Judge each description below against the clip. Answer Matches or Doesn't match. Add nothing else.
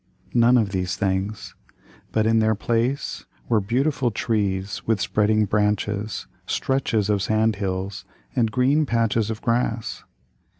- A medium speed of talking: Doesn't match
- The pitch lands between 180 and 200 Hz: Doesn't match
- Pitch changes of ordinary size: Doesn't match